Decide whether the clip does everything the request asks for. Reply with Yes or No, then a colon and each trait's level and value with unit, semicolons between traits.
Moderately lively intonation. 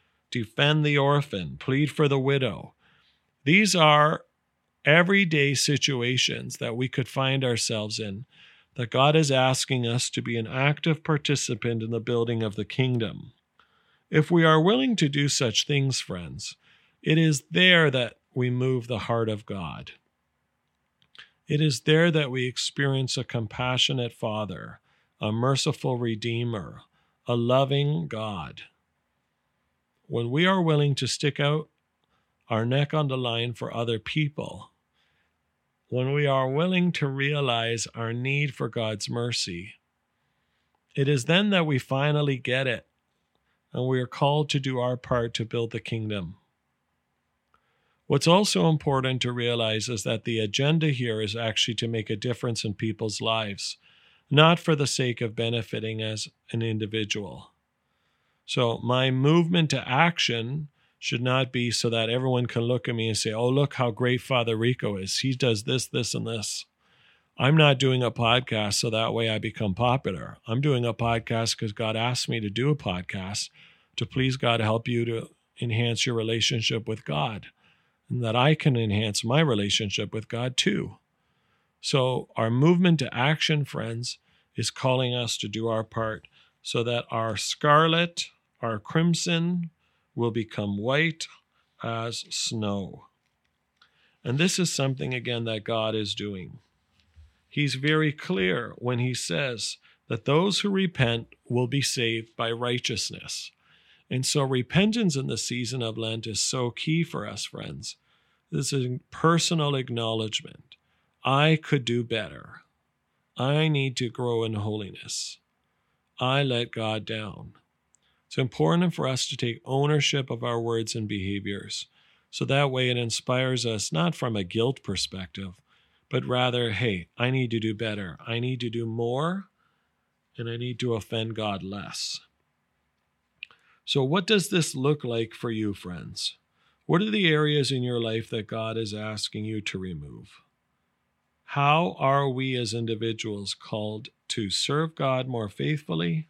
Yes: average, 4.1 semitones